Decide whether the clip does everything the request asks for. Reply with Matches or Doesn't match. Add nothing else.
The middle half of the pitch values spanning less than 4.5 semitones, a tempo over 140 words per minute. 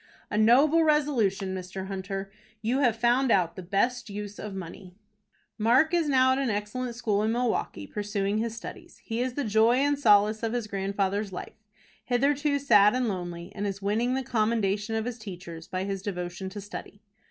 Matches